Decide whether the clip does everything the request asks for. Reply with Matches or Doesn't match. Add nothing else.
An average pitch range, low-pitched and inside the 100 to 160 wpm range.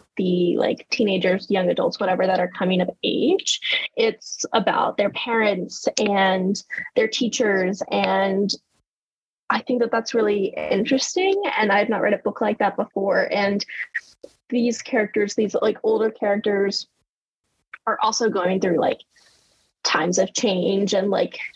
Doesn't match